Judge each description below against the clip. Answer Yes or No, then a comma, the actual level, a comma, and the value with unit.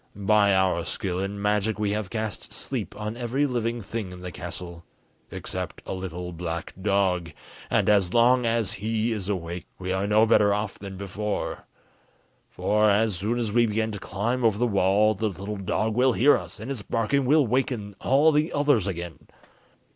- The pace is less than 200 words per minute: Yes, average, 185 wpm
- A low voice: Yes, low, 105 Hz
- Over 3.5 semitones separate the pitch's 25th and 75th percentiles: No, average, 3.2 semitones